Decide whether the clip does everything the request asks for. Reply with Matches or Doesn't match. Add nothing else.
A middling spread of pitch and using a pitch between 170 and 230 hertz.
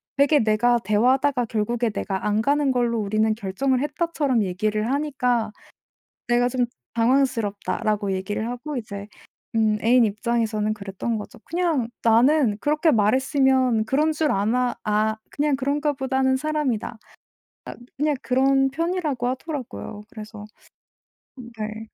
Doesn't match